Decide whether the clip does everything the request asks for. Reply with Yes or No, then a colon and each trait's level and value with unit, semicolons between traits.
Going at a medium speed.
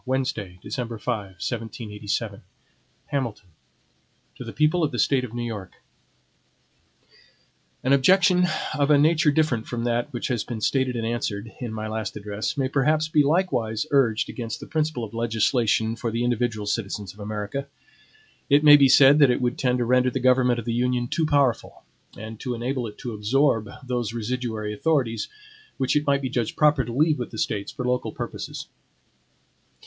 Yes: average, 175 wpm